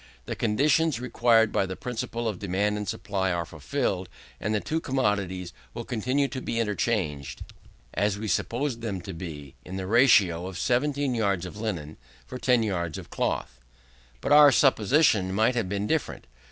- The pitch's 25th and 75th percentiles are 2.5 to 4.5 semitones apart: No, average, 5.0 semitones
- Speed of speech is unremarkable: Yes, average, 170 wpm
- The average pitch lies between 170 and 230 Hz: No, low, 105 Hz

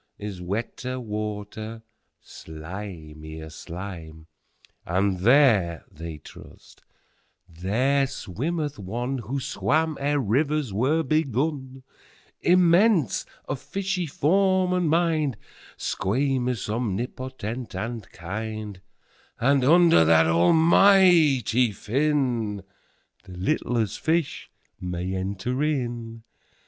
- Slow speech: Yes, slow, 75 wpm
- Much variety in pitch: Yes, wide, 7.1 semitones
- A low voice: Yes, low, 120 Hz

